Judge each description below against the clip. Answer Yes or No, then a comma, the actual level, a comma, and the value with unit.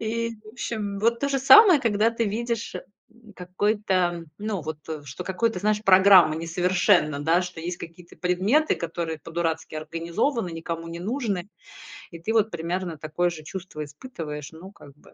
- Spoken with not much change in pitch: No, average, 4.7 semitones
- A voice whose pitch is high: No, medium, 180 Hz